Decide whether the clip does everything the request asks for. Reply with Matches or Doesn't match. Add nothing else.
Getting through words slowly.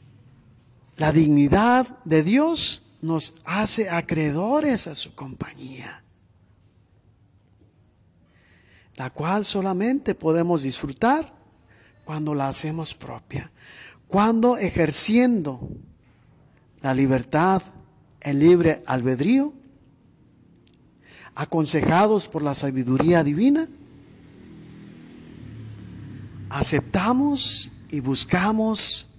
Matches